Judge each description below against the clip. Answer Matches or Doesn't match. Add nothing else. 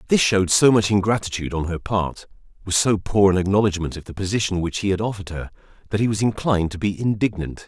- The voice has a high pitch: Doesn't match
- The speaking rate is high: Matches